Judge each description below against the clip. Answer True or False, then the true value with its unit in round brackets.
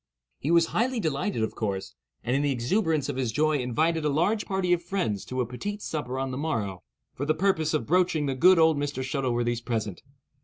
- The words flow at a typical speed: False (215 wpm)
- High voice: False (145 Hz)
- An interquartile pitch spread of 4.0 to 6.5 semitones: True (5.2 semitones)